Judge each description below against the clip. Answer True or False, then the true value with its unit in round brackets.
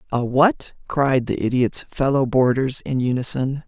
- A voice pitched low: True (130 Hz)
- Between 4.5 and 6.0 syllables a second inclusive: False (4.3 syllables/s)